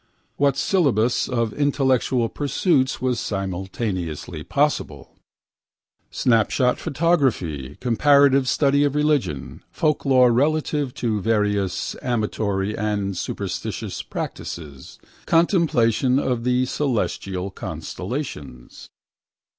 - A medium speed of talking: No, slow, 85 wpm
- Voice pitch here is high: No, low, 125 Hz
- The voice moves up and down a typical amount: No, wide, 5.9 semitones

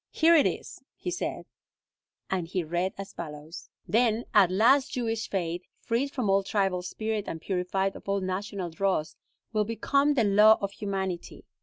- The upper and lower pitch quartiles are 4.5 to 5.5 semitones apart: No, average, 3.6 semitones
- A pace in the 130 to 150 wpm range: No, average, 165 wpm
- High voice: Yes, high, 195 Hz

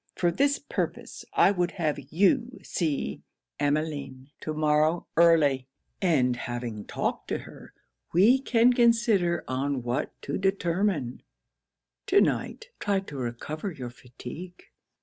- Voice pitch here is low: No, medium, 160 Hz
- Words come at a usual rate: No, slow, 125 wpm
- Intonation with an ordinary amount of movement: No, wide, 6.4 semitones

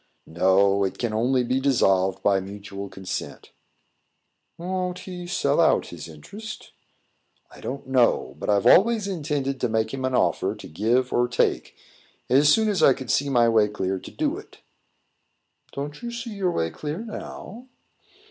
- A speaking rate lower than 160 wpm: No, average, 165 wpm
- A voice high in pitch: No, low, 130 Hz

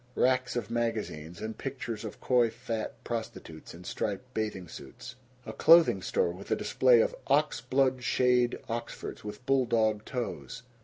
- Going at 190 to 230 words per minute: No, average, 155 wpm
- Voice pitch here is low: Yes, low, 120 Hz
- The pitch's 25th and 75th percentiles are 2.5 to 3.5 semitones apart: Yes, average, 2.8 semitones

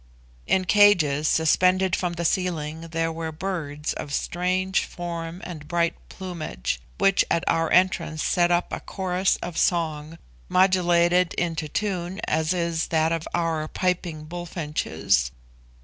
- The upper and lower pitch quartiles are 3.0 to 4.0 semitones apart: No, narrow, 2.4 semitones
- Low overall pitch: No, medium, 170 Hz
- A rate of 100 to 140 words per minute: Yes, slow, 135 wpm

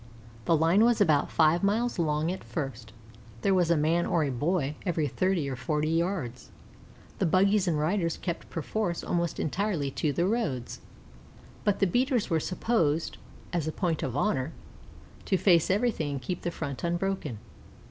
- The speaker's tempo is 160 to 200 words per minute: Yes, average, 170 wpm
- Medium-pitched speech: Yes, medium, 170 Hz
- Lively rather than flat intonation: No, average, 4.2 semitones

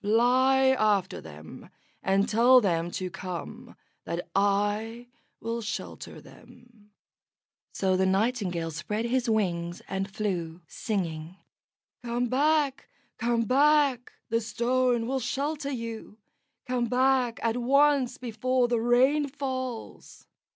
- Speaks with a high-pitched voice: Yes, high, 235 Hz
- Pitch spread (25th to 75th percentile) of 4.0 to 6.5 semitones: Yes, average, 4.4 semitones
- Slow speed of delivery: Yes, slow, 115 wpm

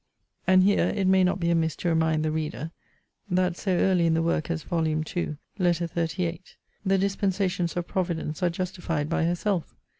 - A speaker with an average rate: Yes, average, 180 wpm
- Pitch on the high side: No, medium, 170 Hz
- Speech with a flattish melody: Yes, narrow, 2.3 semitones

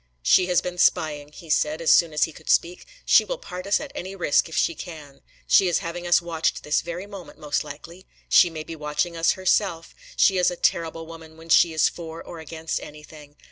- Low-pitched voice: No, medium, 165 Hz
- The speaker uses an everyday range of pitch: No, narrow, 2.2 semitones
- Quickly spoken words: Yes, fast, 220 wpm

